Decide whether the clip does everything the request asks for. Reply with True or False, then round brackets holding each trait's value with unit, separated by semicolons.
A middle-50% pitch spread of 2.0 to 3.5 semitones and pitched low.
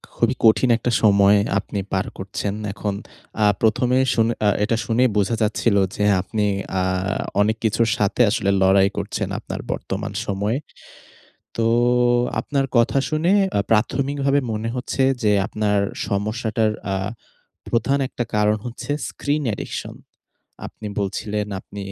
True (2.9 semitones; 110 Hz)